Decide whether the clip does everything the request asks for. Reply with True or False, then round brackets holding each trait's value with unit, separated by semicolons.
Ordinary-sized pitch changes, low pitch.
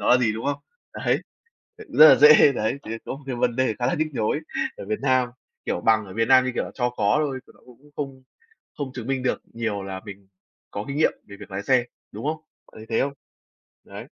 True (3.9 semitones; 125 Hz)